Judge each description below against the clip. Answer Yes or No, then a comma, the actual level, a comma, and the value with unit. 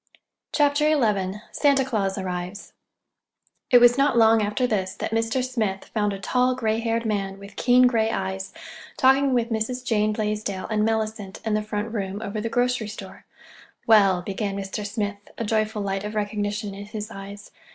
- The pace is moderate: Yes, average, 170 wpm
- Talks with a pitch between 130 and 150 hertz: No, high, 215 Hz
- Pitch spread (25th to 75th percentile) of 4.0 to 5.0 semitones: No, narrow, 2.6 semitones